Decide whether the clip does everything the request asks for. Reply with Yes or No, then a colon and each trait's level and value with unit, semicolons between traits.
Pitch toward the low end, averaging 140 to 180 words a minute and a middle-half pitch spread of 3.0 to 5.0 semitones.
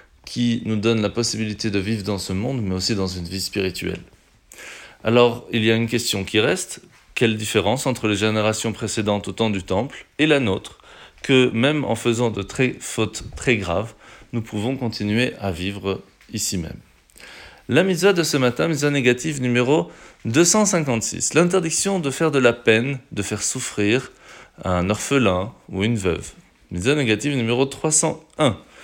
Yes: low, 115 Hz; average, 165 wpm; average, 4.2 semitones